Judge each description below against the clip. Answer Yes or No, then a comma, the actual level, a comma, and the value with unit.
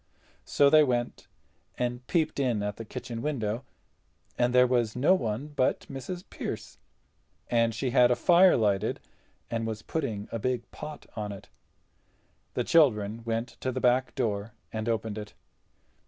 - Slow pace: No, average, 155 wpm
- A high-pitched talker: No, low, 120 Hz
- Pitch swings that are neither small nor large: Yes, average, 3.2 semitones